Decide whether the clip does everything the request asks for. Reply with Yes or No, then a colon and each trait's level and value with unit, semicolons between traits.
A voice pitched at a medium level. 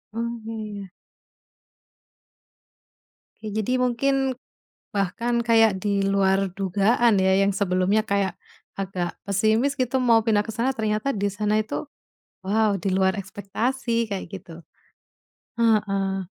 No: high, 210 Hz